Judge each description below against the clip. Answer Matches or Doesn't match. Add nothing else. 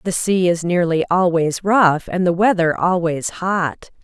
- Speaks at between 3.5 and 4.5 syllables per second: Matches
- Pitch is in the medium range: Matches